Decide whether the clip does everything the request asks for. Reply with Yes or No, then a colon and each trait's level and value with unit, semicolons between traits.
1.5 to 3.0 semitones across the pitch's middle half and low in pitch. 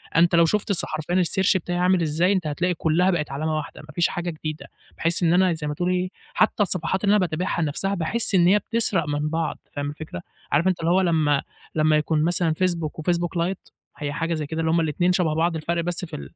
No: narrow, 2.6 semitones; medium, 170 Hz